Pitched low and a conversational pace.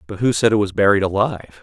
No: low, 100 Hz; fast, 260 wpm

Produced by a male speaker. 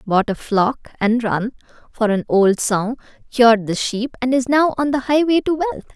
No: female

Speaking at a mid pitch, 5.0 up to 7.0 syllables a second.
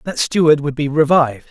Yes: medium, 150 Hz; 5.9 syllables/s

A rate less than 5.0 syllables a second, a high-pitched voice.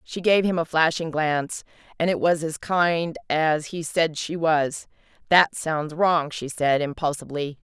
No: 4.2 syllables/s; medium, 160 Hz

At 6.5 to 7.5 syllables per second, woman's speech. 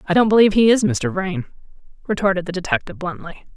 Yes: 6.9 syllables/s; female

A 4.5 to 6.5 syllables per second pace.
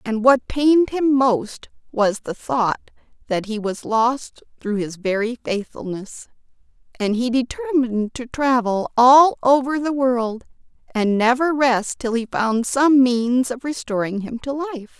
No: 4.0 syllables/s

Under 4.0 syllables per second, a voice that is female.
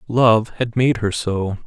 No: 3.5 syllables/s; male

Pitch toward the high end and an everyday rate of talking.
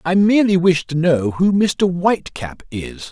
No: medium, 170 Hz; average, 190 wpm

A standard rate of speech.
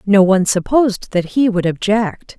Yes: average, 175 wpm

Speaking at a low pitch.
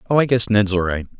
Yes: low, 105 Hz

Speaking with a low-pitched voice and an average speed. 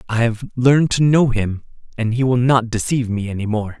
No: low, 120 Hz; fast, 220 wpm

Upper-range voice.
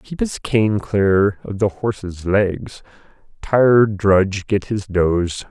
No: low, 100 Hz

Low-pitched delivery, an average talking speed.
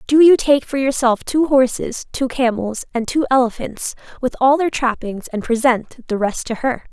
No: very high, 250 Hz; average, 190 wpm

